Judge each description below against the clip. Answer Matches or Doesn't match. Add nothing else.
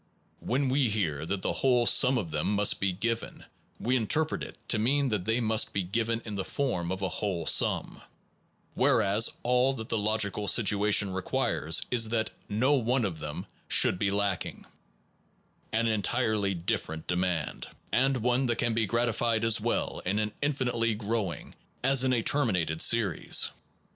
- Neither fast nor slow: Matches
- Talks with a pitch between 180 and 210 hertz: Doesn't match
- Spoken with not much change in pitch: Doesn't match